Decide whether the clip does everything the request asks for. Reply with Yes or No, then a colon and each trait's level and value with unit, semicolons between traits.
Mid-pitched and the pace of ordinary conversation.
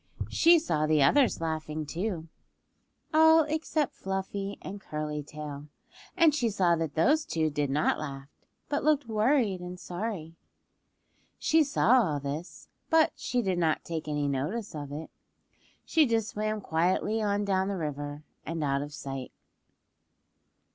Yes: medium, 180 Hz; average, 145 wpm